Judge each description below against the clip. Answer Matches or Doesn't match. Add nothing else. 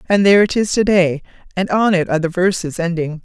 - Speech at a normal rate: Doesn't match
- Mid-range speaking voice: Matches